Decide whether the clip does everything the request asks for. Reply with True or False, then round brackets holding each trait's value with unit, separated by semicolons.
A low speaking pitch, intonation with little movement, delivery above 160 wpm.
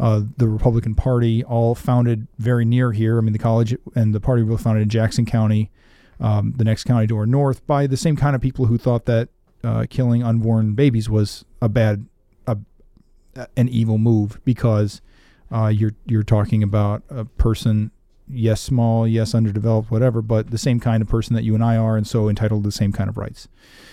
True (115 Hz; 1.7 semitones; 200 wpm)